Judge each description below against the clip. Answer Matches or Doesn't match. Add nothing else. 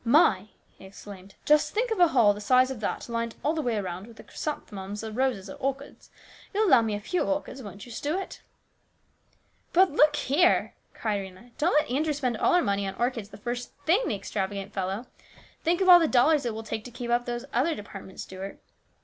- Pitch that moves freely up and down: Matches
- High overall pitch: Matches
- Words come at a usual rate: Doesn't match